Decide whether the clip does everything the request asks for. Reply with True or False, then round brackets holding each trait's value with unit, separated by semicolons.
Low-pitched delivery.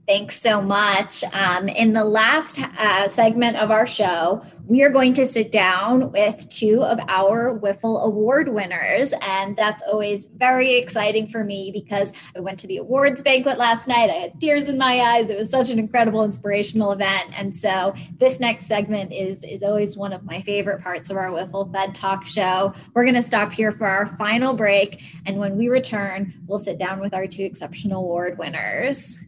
False (205 Hz)